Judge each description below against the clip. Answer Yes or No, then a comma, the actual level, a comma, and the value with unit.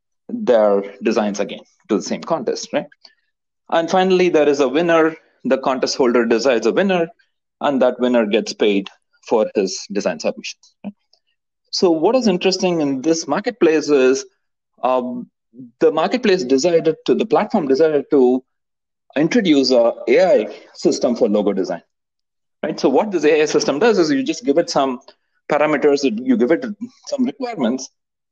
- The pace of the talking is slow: No, average, 155 wpm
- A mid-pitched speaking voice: Yes, medium, 175 Hz